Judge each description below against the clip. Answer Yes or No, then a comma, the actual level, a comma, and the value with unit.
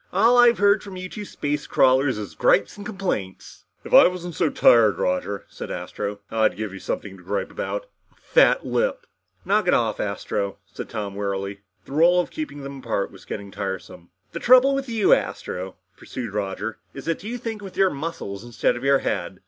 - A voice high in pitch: No, low, 135 Hz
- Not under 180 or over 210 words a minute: Yes, average, 195 wpm